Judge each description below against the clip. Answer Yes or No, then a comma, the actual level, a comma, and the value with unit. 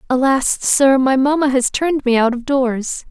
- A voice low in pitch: No, very high, 265 Hz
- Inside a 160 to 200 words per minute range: Yes, average, 195 wpm